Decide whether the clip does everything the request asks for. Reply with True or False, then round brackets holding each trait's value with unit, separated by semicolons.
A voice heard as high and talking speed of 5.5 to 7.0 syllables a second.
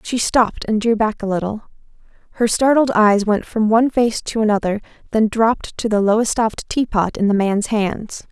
False (220 Hz; 5.1 syllables/s)